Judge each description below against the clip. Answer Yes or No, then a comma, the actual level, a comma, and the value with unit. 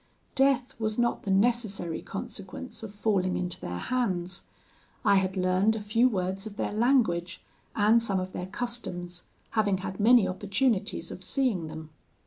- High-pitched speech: Yes, high, 200 Hz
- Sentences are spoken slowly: No, average, 155 wpm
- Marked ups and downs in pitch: No, average, 4.1 semitones